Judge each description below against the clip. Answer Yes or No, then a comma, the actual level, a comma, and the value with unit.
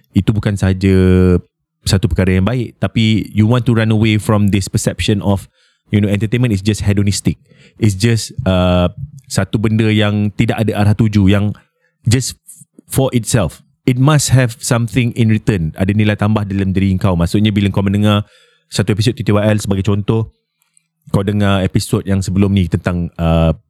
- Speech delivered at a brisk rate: Yes, fast, 165 wpm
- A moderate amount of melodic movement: Yes, average, 3.0 semitones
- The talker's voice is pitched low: Yes, low, 105 Hz